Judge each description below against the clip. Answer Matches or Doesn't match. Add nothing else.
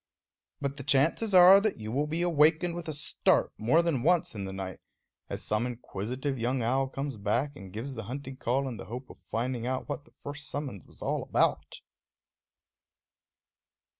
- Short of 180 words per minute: Doesn't match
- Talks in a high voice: Doesn't match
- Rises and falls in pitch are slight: Doesn't match